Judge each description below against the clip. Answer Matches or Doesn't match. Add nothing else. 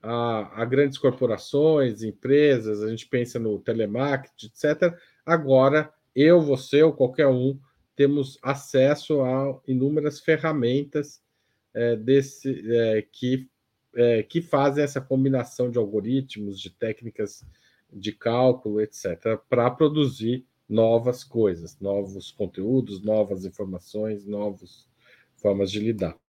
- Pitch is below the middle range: Matches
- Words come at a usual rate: Doesn't match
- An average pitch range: Matches